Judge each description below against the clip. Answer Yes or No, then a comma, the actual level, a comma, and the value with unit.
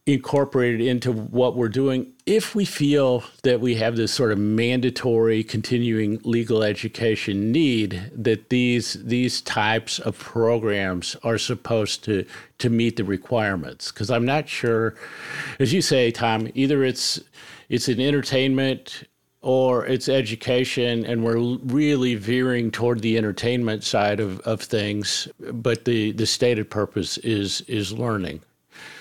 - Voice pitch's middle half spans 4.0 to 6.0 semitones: No, narrow, 2.5 semitones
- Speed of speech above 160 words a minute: No, average, 140 wpm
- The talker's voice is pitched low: Yes, low, 115 Hz